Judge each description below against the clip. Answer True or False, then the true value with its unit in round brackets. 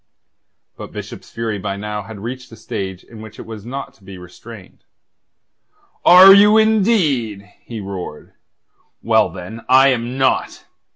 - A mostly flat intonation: False (5.0 semitones)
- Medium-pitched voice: False (115 Hz)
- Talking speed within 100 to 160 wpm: True (150 wpm)